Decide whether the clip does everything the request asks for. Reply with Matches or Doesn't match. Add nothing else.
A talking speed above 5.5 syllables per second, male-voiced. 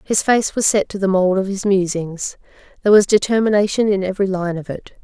Doesn't match